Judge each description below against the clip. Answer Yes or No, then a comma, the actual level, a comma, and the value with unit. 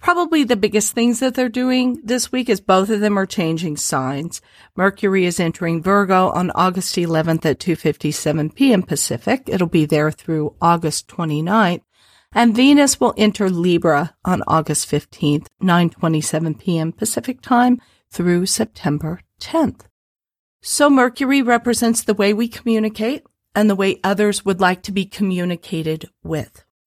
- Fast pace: No, average, 145 wpm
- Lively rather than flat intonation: Yes, wide, 6.0 semitones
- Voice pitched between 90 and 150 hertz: No, high, 190 Hz